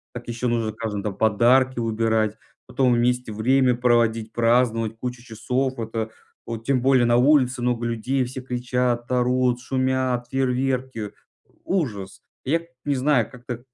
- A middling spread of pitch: No, narrow, 2.2 semitones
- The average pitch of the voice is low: Yes, low, 120 Hz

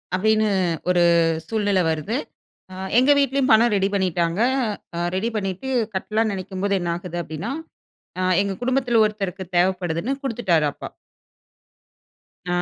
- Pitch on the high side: Yes, high, 195 Hz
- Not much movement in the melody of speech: No, average, 3.7 semitones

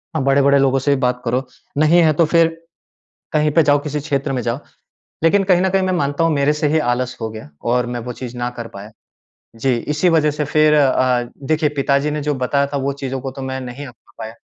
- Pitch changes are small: No, average, 3.0 semitones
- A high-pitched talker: No, medium, 140 Hz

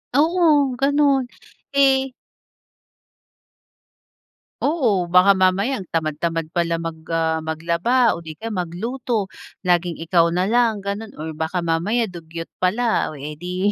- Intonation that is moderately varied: No, wide, 6.5 semitones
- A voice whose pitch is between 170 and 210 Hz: Yes, medium, 185 Hz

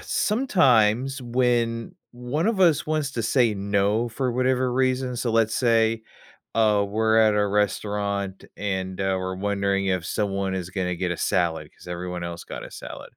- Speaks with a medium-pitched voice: No, low, 110 Hz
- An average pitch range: Yes, average, 4.1 semitones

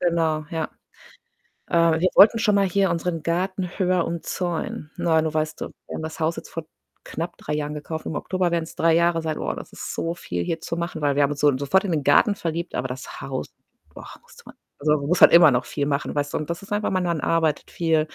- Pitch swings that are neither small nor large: No, narrow, 2.3 semitones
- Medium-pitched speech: Yes, medium, 165 Hz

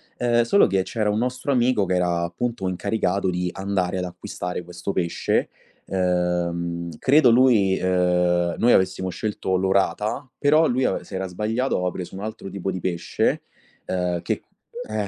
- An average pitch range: Yes, average, 3.9 semitones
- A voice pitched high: No, very low, 95 Hz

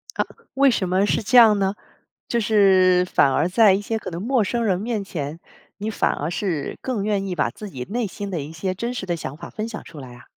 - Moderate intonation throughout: Yes, average, 4.1 semitones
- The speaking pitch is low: No, high, 195 Hz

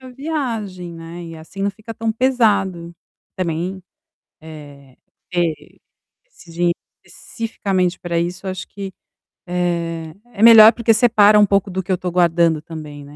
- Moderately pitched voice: Yes, medium, 180 Hz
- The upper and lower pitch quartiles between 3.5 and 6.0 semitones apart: Yes, average, 4.0 semitones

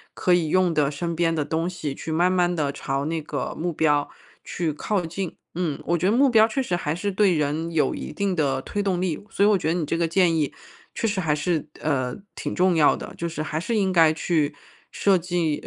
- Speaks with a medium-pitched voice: Yes, medium, 170 Hz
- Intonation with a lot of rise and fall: No, average, 3.1 semitones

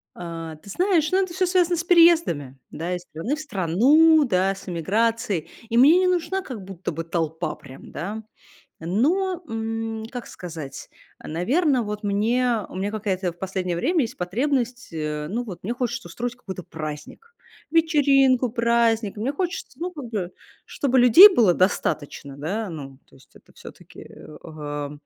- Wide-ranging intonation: Yes, wide, 8.3 semitones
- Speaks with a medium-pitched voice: No, high, 220 Hz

